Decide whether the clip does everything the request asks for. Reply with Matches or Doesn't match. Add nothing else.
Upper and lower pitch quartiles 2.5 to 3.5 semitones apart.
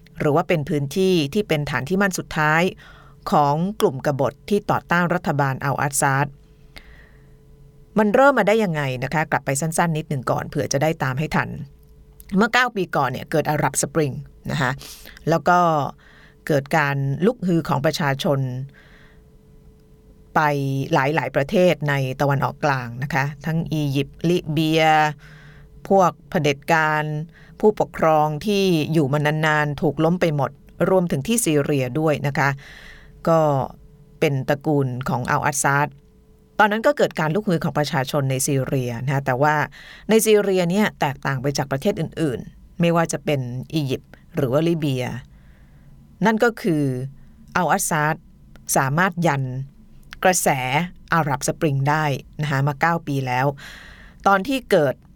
Matches